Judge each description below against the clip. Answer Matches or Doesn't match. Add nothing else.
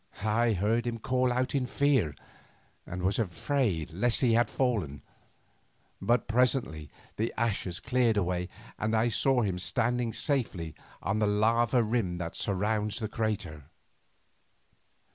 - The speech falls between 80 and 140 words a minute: Matches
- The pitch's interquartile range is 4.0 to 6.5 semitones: Matches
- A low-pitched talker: Matches